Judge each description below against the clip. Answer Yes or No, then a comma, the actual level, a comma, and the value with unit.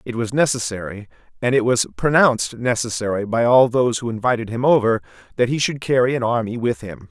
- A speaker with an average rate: Yes, average, 195 wpm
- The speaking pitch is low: Yes, low, 115 Hz